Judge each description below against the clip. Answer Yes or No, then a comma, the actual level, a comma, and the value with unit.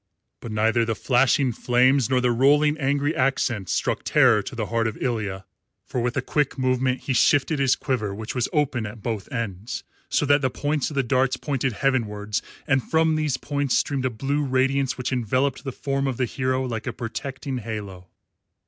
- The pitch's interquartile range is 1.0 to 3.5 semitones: Yes, average, 3.0 semitones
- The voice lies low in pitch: Yes, low, 130 Hz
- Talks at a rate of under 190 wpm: No, average, 195 wpm